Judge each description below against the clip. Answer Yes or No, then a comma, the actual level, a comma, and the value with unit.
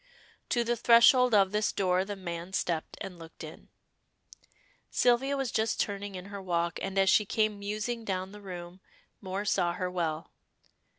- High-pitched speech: Yes, high, 195 Hz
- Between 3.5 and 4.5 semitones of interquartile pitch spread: No, average, 3.0 semitones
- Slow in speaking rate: No, average, 170 wpm